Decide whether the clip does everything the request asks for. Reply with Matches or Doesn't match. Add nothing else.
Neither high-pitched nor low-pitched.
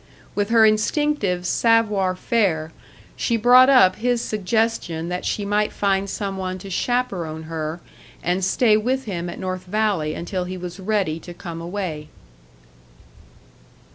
Doesn't match